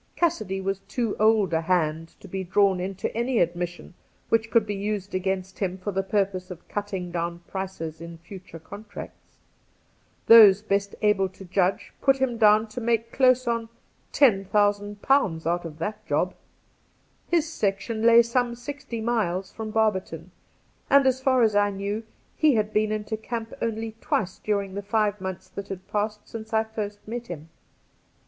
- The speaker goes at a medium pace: Yes, average, 170 wpm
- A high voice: Yes, high, 205 Hz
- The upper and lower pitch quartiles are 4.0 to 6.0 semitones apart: No, average, 3.2 semitones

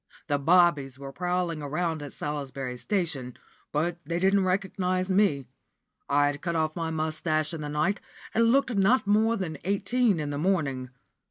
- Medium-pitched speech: Yes, medium, 165 Hz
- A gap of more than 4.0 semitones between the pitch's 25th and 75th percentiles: Yes, average, 4.7 semitones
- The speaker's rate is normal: Yes, average, 160 wpm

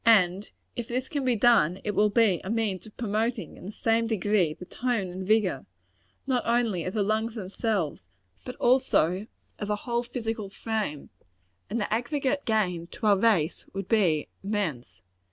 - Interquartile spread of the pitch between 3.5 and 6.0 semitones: Yes, average, 3.8 semitones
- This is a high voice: Yes, high, 215 Hz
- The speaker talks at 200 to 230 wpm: No, average, 170 wpm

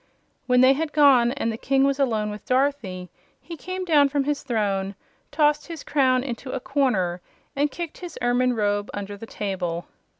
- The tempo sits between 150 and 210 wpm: Yes, average, 180 wpm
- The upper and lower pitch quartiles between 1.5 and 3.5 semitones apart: No, wide, 5.5 semitones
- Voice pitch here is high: Yes, very high, 255 Hz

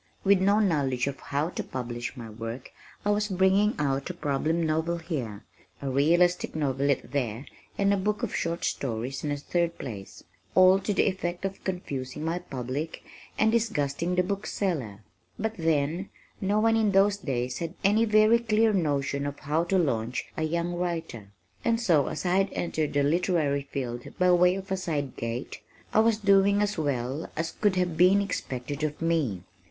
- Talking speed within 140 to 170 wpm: No, average, 180 wpm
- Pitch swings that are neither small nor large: No, wide, 5.7 semitones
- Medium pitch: Yes, medium, 165 Hz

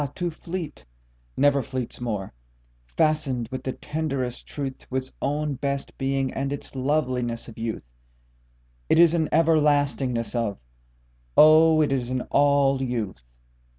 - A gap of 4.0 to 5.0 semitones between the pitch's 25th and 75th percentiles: No, average, 3.5 semitones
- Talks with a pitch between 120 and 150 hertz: Yes, low, 135 Hz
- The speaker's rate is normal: No, slow, 125 wpm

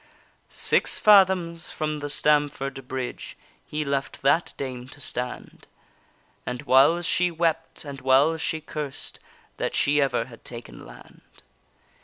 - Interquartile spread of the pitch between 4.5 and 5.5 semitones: No, average, 3.5 semitones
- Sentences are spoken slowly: Yes, slow, 130 wpm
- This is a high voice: No, medium, 145 Hz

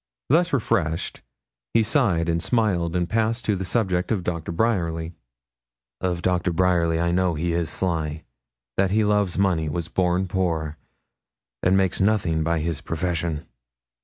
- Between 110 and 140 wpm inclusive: No, average, 155 wpm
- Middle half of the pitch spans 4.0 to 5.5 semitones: No, average, 2.7 semitones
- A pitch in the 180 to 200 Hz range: No, very low, 90 Hz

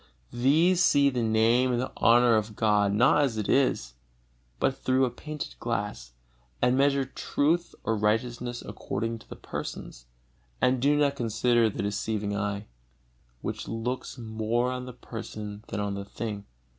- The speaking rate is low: No, average, 155 wpm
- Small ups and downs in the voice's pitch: No, average, 3.4 semitones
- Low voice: Yes, low, 115 Hz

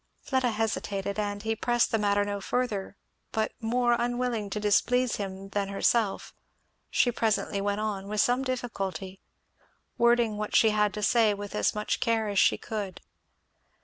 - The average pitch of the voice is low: No, high, 215 Hz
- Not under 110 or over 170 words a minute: Yes, average, 160 wpm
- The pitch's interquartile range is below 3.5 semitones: Yes, average, 2.8 semitones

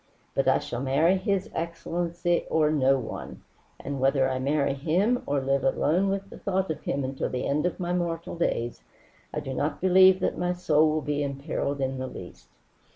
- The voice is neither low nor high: Yes, medium, 155 Hz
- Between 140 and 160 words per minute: No, average, 195 wpm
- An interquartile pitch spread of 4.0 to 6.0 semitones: Yes, average, 4.5 semitones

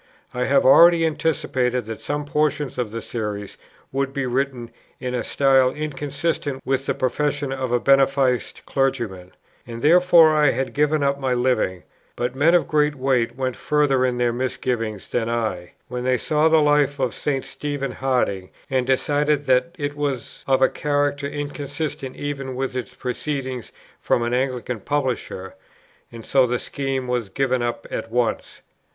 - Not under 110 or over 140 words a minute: No, average, 165 wpm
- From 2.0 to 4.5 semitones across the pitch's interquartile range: Yes, average, 2.8 semitones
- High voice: No, low, 135 Hz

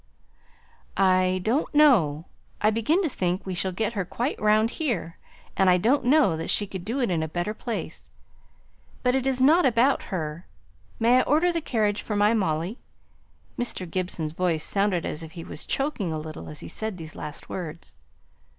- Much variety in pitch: Yes, wide, 6.0 semitones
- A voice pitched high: Yes, high, 200 Hz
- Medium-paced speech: Yes, average, 180 wpm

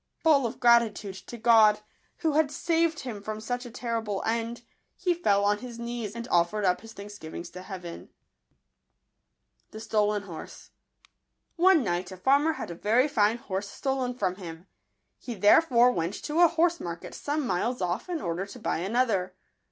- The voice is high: Yes, high, 225 Hz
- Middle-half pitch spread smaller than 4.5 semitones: No, average, 4.8 semitones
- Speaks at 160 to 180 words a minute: Yes, average, 175 wpm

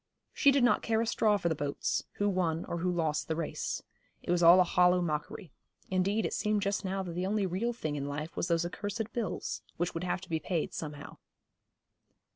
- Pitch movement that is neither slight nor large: Yes, average, 3.7 semitones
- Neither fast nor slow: No, fast, 220 wpm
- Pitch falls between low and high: Yes, medium, 180 Hz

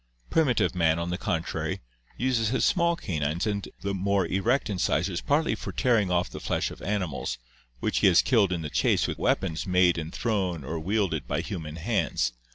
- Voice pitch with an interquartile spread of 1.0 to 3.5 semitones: No, average, 4.4 semitones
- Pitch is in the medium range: No, very low, 95 Hz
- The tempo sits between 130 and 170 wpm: No, average, 180 wpm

